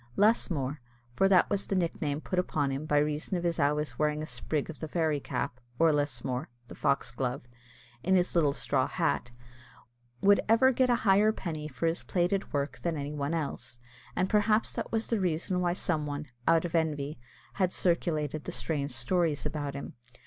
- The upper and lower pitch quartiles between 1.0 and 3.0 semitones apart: No, average, 4.0 semitones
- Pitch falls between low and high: Yes, medium, 155 Hz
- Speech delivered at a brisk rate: No, average, 185 wpm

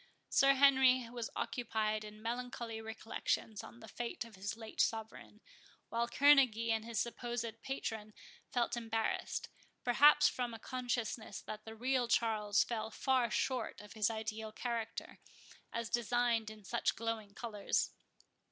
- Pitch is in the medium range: No, high, 230 Hz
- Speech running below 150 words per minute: Yes, average, 140 wpm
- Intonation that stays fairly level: Yes, narrow, 1.8 semitones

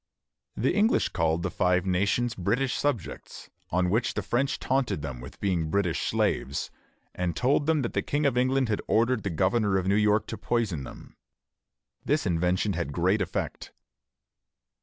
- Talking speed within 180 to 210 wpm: No, average, 165 wpm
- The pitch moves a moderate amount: No, wide, 5.8 semitones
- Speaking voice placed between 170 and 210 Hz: No, low, 100 Hz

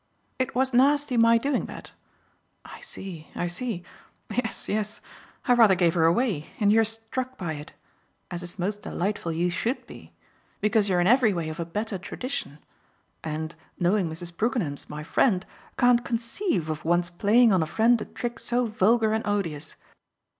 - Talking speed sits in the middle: Yes, average, 170 wpm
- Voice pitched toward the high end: Yes, high, 205 Hz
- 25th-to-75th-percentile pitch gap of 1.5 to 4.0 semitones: No, wide, 5.4 semitones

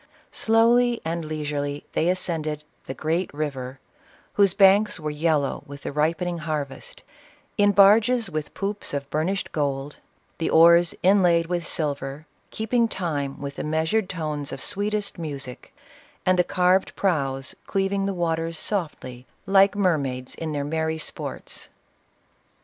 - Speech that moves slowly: No, average, 145 wpm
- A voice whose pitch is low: No, medium, 165 Hz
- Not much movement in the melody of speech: No, average, 4.8 semitones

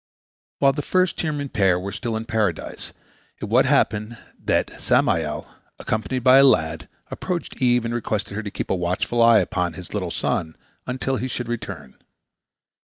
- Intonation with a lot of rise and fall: Yes, wide, 5.8 semitones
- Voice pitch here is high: No, low, 115 Hz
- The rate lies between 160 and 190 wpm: Yes, average, 165 wpm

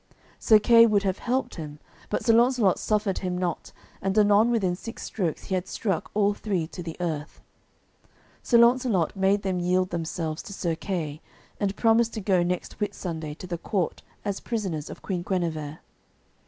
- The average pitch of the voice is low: No, high, 190 Hz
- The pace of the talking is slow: No, average, 175 wpm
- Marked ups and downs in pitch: No, average, 3.6 semitones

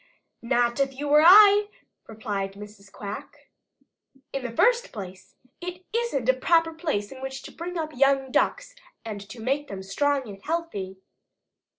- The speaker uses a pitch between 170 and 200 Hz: No, very high, 265 Hz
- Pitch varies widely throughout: Yes, wide, 8.0 semitones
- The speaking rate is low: No, average, 155 wpm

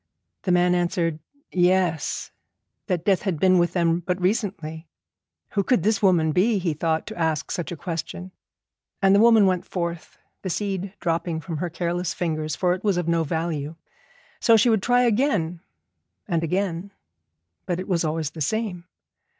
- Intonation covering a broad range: No, average, 2.8 semitones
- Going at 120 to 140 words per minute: No, average, 170 wpm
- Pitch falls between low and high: Yes, medium, 175 Hz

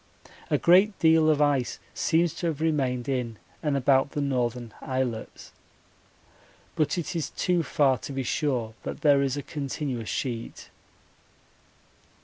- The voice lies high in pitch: No, medium, 140 Hz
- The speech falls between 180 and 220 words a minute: No, average, 140 wpm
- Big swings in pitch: No, average, 3.8 semitones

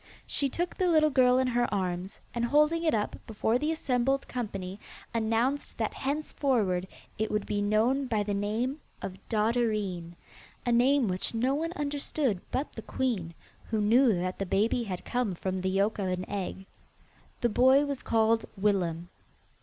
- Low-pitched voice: No, high, 225 Hz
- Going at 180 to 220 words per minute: No, average, 170 wpm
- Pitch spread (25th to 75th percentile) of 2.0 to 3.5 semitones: No, average, 5.0 semitones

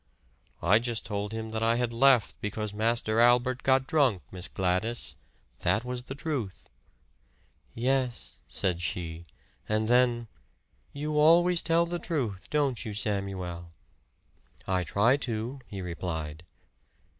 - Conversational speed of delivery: No, slow, 130 wpm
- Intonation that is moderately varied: Yes, average, 5.0 semitones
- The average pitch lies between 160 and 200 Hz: No, low, 115 Hz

